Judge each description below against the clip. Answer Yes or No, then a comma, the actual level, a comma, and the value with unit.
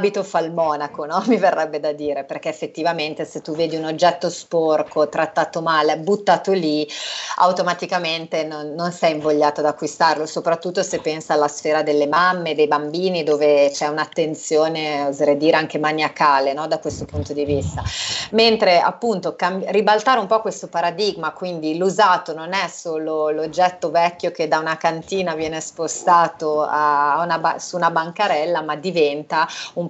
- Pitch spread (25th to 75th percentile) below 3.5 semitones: Yes, narrow, 2.6 semitones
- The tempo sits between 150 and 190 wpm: Yes, average, 160 wpm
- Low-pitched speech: No, medium, 160 Hz